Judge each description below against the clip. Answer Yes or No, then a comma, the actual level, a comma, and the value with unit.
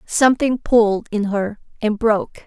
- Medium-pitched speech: No, high, 220 Hz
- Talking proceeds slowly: Yes, slow, 120 wpm